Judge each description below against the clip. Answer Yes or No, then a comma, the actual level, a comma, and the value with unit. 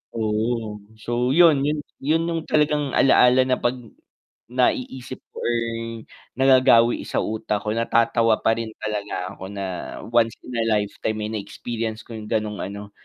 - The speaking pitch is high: No, low, 115 Hz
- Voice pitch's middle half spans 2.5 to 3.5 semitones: Yes, average, 3.2 semitones